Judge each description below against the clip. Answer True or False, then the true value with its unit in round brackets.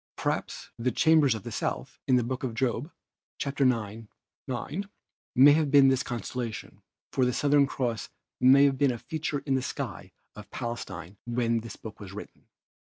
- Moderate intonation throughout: True (3.3 semitones)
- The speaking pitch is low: True (125 Hz)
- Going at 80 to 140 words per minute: False (165 wpm)